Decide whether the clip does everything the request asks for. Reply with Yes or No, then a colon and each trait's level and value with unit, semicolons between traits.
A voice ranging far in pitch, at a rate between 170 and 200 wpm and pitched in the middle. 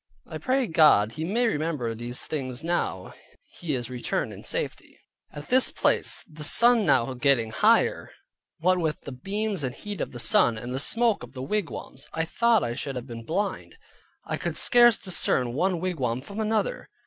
Yes: wide, 8.5 semitones; average, 185 wpm; medium, 155 Hz